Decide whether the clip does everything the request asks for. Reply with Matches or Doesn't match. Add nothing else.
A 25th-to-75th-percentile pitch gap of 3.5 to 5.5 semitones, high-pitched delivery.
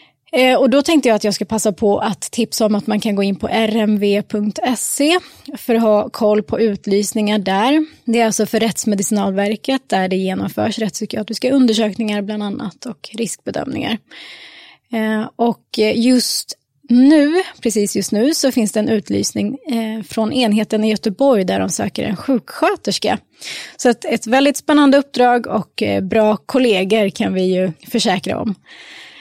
Doesn't match